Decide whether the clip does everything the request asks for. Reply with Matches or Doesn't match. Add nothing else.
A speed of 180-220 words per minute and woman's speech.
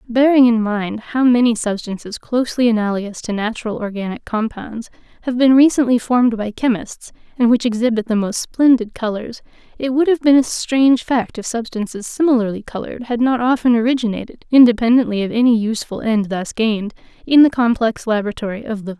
Doesn't match